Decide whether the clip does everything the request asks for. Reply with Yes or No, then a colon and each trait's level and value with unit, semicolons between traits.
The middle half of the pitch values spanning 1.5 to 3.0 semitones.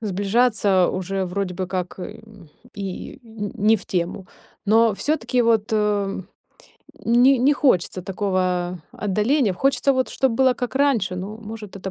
No: average, 4.0 semitones